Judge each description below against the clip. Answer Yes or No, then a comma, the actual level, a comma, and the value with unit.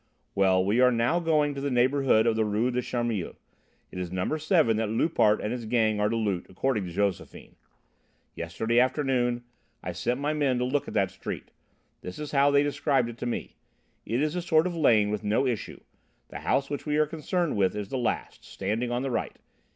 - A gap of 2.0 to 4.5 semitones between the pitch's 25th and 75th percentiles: No, average, 5.1 semitones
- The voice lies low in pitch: Yes, low, 120 Hz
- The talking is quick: Yes, fast, 215 wpm